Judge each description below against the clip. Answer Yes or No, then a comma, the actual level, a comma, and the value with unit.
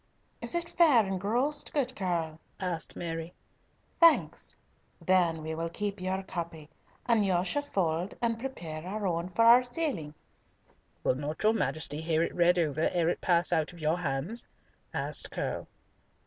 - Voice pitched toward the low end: No, medium, 180 Hz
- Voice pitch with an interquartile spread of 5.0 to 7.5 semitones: Yes, wide, 5.5 semitones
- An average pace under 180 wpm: Yes, average, 160 wpm